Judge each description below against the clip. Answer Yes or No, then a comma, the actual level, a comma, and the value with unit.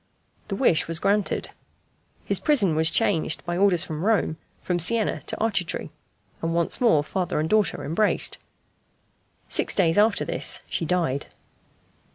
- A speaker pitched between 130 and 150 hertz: No, medium, 180 Hz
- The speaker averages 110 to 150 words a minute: Yes, average, 145 wpm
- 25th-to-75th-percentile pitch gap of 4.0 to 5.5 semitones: Yes, average, 4.3 semitones